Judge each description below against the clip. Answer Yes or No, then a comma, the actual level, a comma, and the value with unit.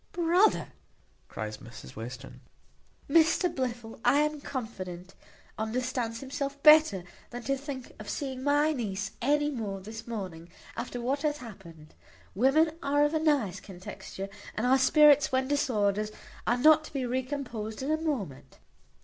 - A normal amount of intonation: No, wide, 5.9 semitones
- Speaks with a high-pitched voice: Yes, very high, 255 Hz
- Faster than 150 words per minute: No, average, 145 wpm